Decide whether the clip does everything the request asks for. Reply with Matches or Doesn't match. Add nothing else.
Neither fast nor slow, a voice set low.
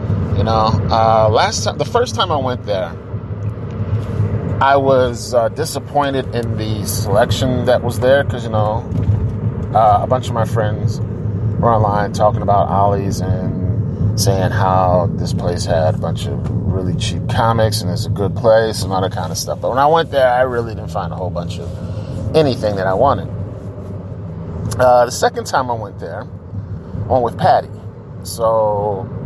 Matches